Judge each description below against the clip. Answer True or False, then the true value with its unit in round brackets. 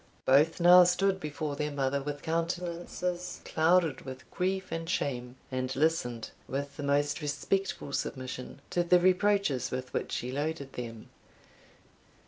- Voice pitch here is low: False (150 Hz)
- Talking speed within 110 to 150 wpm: True (135 wpm)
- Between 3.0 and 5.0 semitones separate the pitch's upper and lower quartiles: True (4.7 semitones)